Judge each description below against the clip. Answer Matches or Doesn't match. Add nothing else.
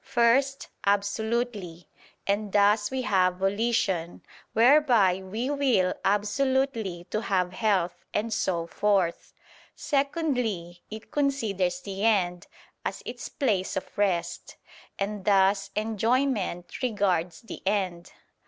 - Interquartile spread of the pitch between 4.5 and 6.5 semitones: Doesn't match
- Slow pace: Matches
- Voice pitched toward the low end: Doesn't match